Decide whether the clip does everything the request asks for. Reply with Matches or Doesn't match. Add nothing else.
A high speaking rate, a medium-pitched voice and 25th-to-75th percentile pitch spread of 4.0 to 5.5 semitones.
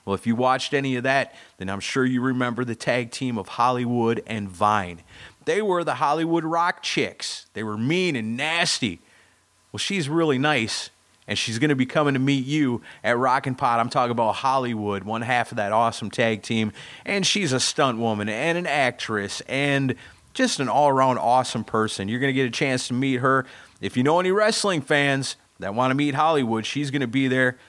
Doesn't match